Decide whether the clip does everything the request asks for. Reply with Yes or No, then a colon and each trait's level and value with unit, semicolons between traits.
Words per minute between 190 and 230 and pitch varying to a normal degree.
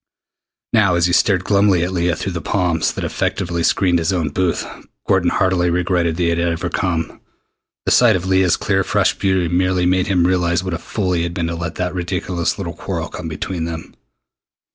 No: fast, 205 wpm; narrow, 1.6 semitones